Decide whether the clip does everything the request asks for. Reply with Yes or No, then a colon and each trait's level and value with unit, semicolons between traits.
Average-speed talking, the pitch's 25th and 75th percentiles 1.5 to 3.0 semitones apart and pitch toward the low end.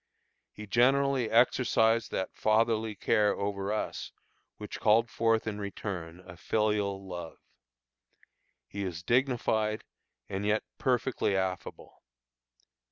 No: slow, 105 wpm; average, 2.7 semitones; low, 105 Hz